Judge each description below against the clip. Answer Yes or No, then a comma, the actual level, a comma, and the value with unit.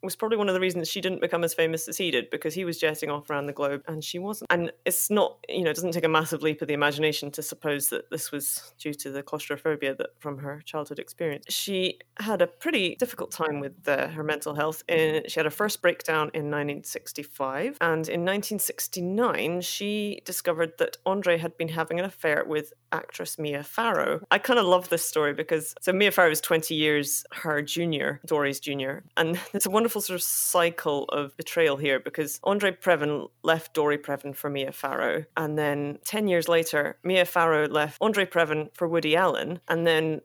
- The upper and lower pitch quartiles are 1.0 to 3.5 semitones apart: Yes, average, 3.2 semitones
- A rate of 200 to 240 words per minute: Yes, fast, 205 wpm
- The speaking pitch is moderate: Yes, medium, 160 Hz